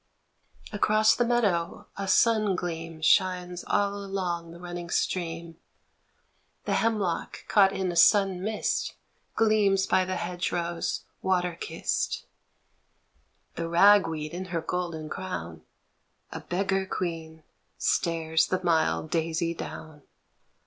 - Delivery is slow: Yes, slow, 120 wpm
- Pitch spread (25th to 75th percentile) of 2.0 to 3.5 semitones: Yes, average, 2.7 semitones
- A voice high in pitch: No, medium, 180 Hz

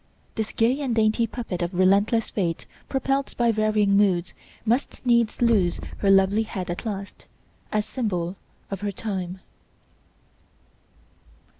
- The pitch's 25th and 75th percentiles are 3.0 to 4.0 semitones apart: Yes, average, 3.4 semitones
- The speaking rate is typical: No, slow, 130 wpm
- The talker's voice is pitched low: No, high, 210 Hz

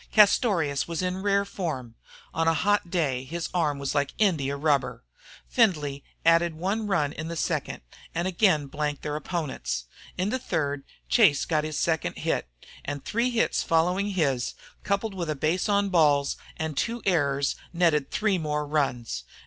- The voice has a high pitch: No, medium, 160 Hz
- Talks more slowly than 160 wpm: No, average, 165 wpm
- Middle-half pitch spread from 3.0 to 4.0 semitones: No, average, 4.7 semitones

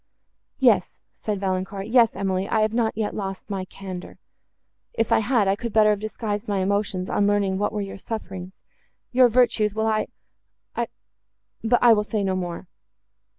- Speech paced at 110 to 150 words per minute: No, average, 160 wpm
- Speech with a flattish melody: Yes, narrow, 2.3 semitones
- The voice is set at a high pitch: Yes, high, 205 Hz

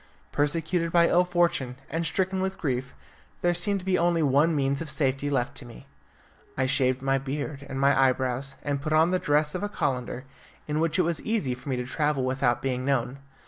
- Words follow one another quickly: Yes, fast, 210 wpm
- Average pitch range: Yes, average, 4.1 semitones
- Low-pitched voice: No, medium, 145 Hz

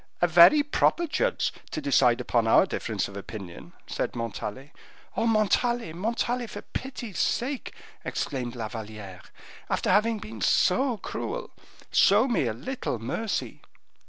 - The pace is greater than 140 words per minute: No, slow, 135 wpm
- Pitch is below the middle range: No, medium, 175 Hz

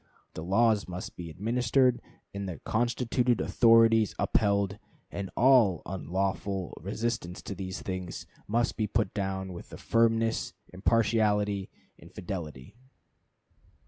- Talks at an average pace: No, slow, 110 wpm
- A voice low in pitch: Yes, low, 100 Hz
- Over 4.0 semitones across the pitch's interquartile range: No, average, 3.4 semitones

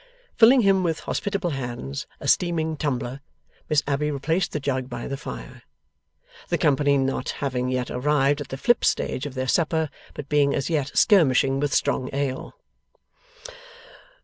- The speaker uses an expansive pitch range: No, average, 3.4 semitones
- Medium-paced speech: Yes, average, 155 wpm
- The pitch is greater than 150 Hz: No, medium, 140 Hz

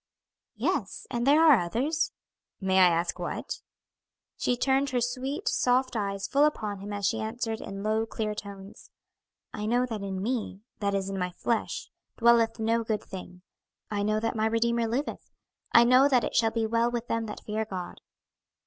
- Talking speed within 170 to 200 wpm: Yes, average, 185 wpm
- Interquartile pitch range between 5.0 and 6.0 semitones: No, average, 3.2 semitones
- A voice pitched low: No, high, 225 Hz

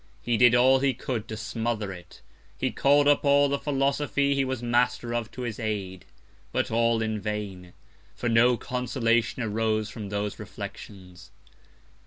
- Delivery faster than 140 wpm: Yes, average, 160 wpm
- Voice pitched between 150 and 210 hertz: No, low, 115 Hz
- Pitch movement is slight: No, average, 3.4 semitones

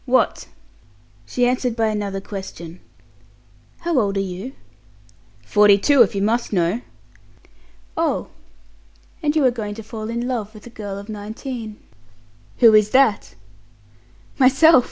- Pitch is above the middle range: Yes, high, 220 Hz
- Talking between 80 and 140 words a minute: Yes, slow, 135 wpm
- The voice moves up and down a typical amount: Yes, average, 3.4 semitones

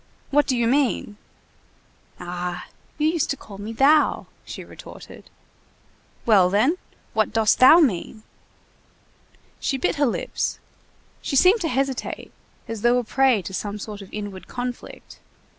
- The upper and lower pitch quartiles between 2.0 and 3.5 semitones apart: No, average, 5.1 semitones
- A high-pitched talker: Yes, high, 235 Hz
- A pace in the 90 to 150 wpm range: Yes, average, 140 wpm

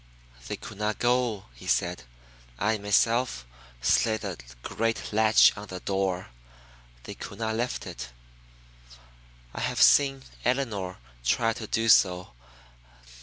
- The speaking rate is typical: No, slow, 125 wpm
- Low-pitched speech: Yes, low, 110 Hz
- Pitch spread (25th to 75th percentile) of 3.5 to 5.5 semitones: No, average, 3.1 semitones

